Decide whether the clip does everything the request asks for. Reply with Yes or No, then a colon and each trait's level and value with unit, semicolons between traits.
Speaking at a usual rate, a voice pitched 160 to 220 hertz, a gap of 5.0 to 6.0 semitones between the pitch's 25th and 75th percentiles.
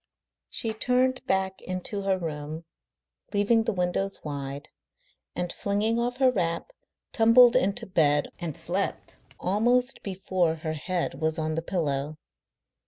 No: slow, 130 wpm; medium, 185 Hz; wide, 5.5 semitones